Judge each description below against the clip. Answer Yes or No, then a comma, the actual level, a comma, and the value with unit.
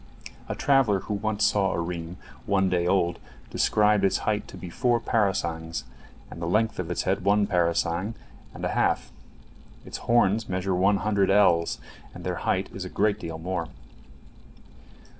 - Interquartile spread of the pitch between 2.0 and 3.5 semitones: Yes, average, 3.2 semitones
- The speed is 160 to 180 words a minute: Yes, average, 165 wpm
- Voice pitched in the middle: No, very low, 95 Hz